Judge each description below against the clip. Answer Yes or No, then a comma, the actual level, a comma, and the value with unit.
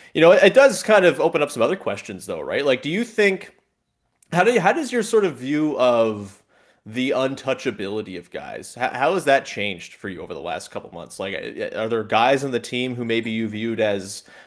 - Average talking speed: No, fast, 230 wpm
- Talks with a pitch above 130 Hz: No, low, 125 Hz